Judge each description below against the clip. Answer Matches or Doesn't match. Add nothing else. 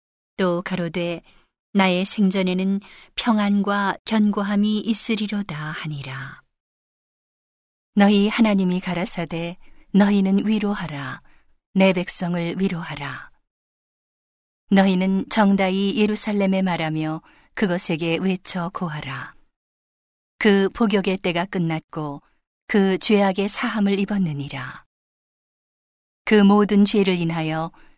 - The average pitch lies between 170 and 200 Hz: Matches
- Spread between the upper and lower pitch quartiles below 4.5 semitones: Matches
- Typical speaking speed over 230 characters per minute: Doesn't match